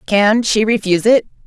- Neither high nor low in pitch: No, high, 210 Hz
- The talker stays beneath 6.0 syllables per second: Yes, 5.1 syllables/s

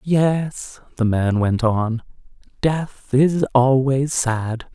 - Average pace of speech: No, slow, 115 wpm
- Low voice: Yes, low, 130 Hz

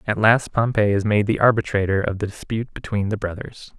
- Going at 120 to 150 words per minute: No, fast, 205 wpm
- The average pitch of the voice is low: Yes, low, 105 Hz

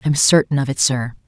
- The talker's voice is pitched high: No, low, 135 Hz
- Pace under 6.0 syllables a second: Yes, 5.5 syllables/s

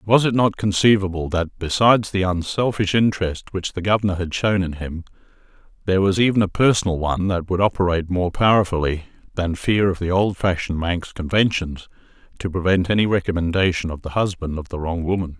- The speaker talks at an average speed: Yes, average, 180 wpm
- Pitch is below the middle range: Yes, very low, 95 Hz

